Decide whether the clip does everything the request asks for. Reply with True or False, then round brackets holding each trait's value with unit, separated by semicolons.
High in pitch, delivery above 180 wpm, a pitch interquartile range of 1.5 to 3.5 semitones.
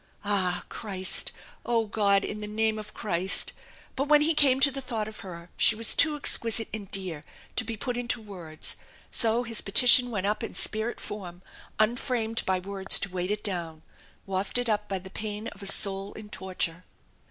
True (210 Hz; 190 wpm; 3.2 semitones)